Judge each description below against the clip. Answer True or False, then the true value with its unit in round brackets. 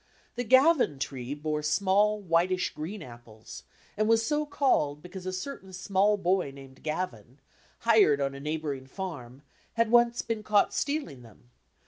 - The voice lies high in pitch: False (180 Hz)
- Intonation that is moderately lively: False (7.3 semitones)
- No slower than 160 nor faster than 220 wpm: False (150 wpm)